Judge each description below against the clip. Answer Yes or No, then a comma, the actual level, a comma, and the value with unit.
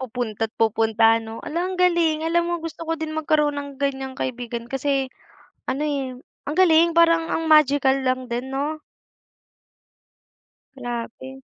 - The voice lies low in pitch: No, very high, 275 Hz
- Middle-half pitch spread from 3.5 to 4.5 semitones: Yes, average, 4.2 semitones